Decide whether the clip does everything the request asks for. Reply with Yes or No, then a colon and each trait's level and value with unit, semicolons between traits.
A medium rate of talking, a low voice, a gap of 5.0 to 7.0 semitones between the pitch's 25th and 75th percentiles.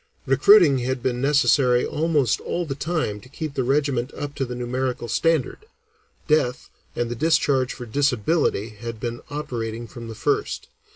No: average, 160 wpm; low, 130 Hz; average, 3.5 semitones